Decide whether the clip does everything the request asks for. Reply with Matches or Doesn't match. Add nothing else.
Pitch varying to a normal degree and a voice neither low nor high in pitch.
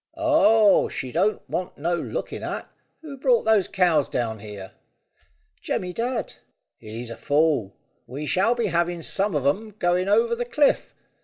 Doesn't match